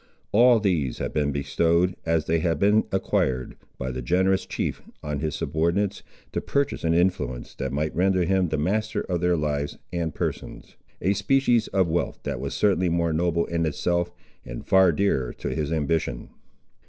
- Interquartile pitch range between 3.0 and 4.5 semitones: Yes, average, 3.9 semitones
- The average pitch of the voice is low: Yes, very low, 85 Hz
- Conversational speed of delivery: Yes, average, 175 wpm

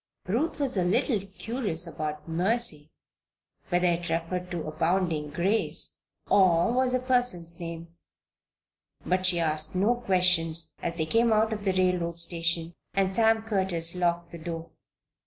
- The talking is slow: No, average, 145 wpm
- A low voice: No, medium, 180 Hz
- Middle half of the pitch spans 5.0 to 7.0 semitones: No, average, 3.9 semitones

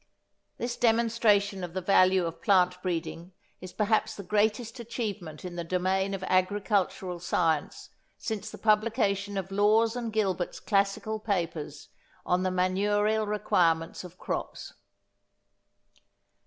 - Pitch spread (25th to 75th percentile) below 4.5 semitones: Yes, average, 3.0 semitones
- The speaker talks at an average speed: No, slow, 125 wpm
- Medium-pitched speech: No, high, 195 Hz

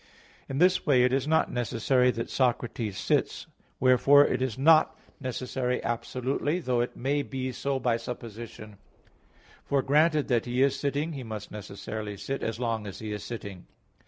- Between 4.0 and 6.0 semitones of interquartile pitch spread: No, average, 3.3 semitones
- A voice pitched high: No, low, 125 Hz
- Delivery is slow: No, average, 165 wpm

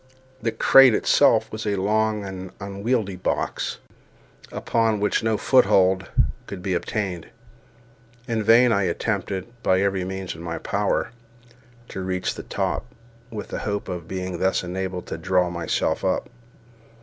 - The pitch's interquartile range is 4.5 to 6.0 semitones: No, average, 2.8 semitones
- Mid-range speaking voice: No, very low, 95 Hz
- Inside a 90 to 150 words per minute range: Yes, average, 145 wpm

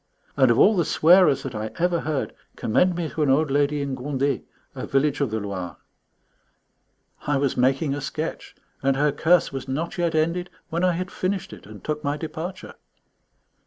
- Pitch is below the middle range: No, medium, 145 Hz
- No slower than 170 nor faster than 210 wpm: Yes, average, 190 wpm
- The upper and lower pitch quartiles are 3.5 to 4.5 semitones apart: Yes, average, 3.8 semitones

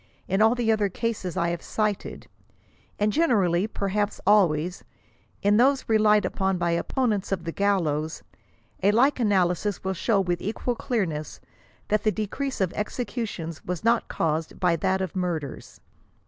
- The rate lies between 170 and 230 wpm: No, average, 150 wpm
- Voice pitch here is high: Yes, high, 200 Hz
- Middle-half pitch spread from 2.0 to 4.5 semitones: Yes, average, 3.8 semitones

